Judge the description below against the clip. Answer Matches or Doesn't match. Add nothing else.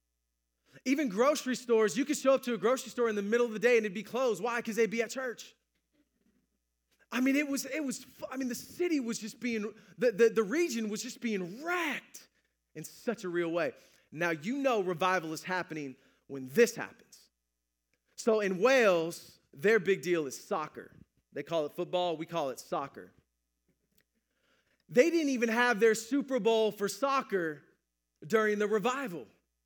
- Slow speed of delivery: Doesn't match